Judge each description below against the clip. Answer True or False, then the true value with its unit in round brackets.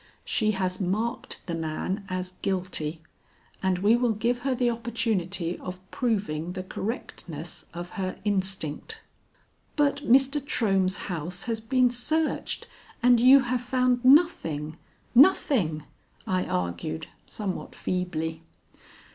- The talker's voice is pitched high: True (195 Hz)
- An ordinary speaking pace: False (120 wpm)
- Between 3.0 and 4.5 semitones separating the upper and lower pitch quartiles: False (5.5 semitones)